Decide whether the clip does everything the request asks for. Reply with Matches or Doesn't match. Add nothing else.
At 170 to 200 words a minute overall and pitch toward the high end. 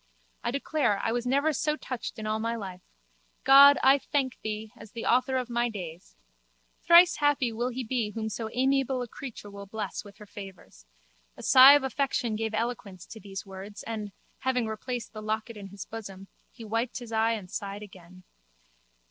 Matches